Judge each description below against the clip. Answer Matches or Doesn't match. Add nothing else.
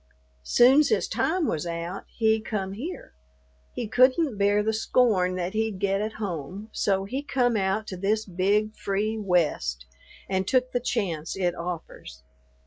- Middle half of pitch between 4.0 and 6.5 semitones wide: Doesn't match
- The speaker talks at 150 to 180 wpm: Matches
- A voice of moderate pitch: Doesn't match